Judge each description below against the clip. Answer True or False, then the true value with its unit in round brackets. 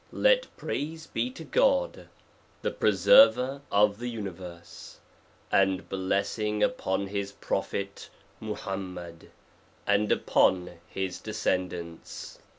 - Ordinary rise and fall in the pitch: True (3.6 semitones)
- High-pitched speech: False (100 Hz)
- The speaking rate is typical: False (100 wpm)